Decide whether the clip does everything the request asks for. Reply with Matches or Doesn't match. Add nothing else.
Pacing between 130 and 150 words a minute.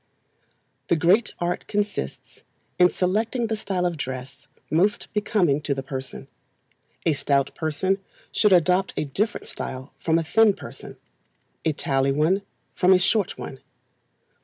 Matches